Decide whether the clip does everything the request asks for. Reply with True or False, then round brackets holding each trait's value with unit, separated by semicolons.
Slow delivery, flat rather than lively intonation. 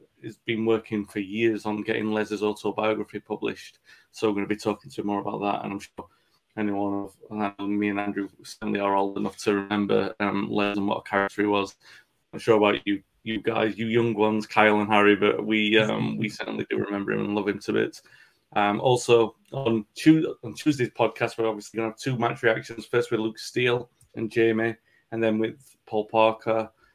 False (205 wpm; 1.7 semitones)